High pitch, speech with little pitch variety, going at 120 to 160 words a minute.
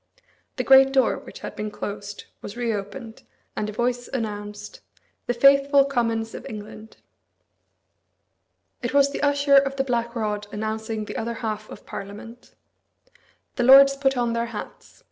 No: high, 235 Hz; average, 4.1 semitones; average, 150 wpm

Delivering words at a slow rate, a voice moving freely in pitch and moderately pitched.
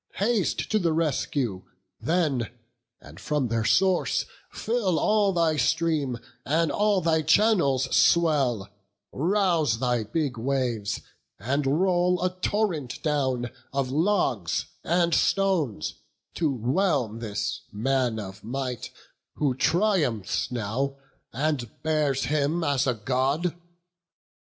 Yes: slow, 115 wpm; wide, 5.7 semitones; medium, 145 Hz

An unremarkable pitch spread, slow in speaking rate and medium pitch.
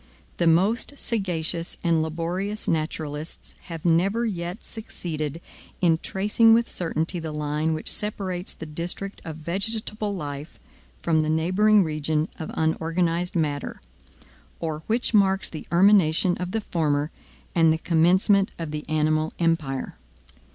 Yes: average, 3.5 semitones; slow, 130 wpm; medium, 170 Hz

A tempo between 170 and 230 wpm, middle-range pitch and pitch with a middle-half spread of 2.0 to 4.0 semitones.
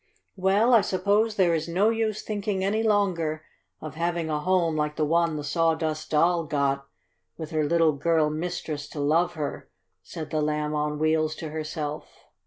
Yes: average, 175 wpm; medium, 160 Hz; average, 3.1 semitones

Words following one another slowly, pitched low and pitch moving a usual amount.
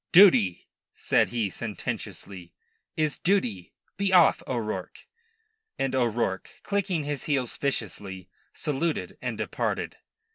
No: slow, 105 wpm; low, 125 Hz; wide, 7.8 semitones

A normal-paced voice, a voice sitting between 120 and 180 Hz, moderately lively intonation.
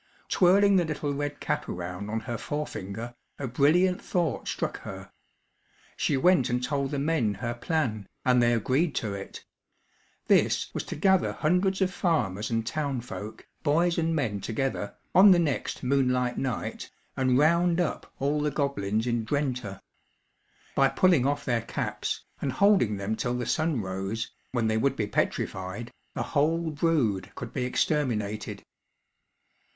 No: average, 155 wpm; low, 135 Hz; wide, 5.8 semitones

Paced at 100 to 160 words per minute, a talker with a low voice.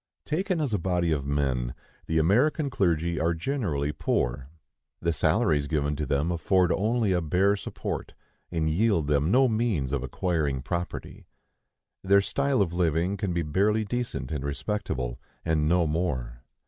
Yes: average, 155 wpm; very low, 85 Hz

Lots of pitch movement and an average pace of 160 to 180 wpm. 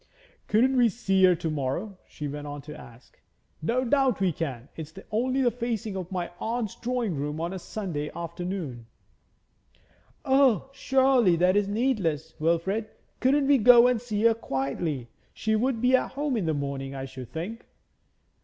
Yes: wide, 7.7 semitones; average, 170 wpm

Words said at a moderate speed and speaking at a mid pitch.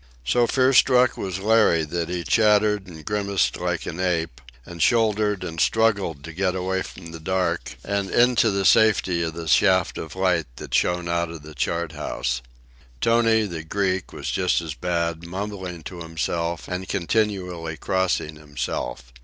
No: average, 165 wpm; very low, 90 Hz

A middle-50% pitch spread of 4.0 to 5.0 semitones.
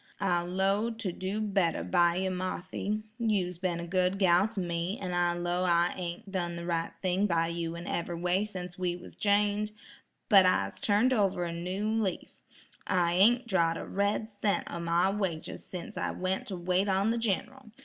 No: average, 2.7 semitones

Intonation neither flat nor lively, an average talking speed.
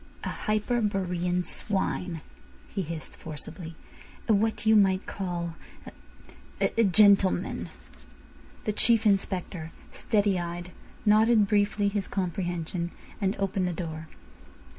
No: average, 3.1 semitones; slow, 105 wpm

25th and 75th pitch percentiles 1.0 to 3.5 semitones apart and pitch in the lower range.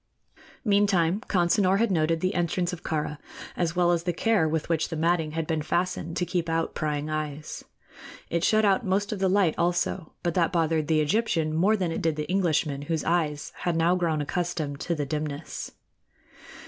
No: average, 2.7 semitones; medium, 170 Hz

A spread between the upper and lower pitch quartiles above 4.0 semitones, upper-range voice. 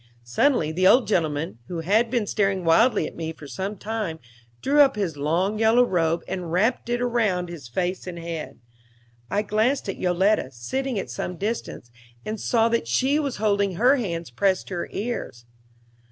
Yes: average, 5.3 semitones; high, 195 Hz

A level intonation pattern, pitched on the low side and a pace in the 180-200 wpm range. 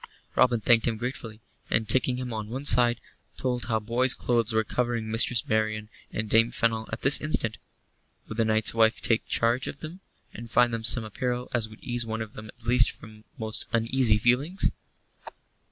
Yes: narrow, 2.0 semitones; low, 115 Hz; average, 185 wpm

